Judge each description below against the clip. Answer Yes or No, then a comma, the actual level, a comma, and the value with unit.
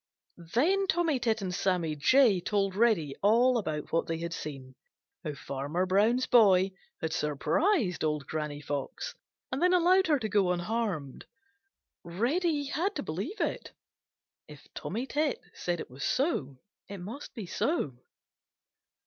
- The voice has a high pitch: Yes, high, 195 Hz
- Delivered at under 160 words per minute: Yes, average, 145 wpm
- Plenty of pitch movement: Yes, wide, 8.8 semitones